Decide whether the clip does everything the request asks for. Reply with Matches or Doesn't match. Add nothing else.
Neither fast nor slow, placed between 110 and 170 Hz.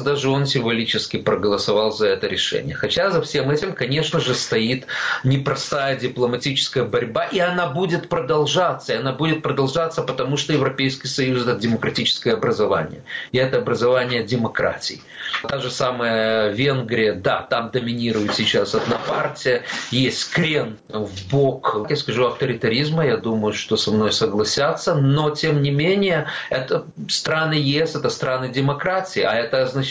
Matches